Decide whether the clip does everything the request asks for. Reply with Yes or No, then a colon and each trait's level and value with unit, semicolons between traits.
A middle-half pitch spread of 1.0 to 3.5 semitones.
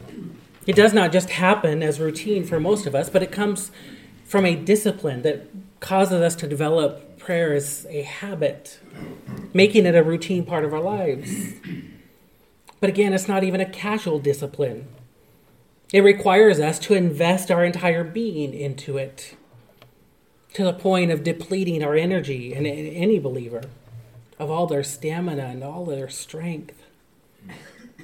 No: average, 4.8 semitones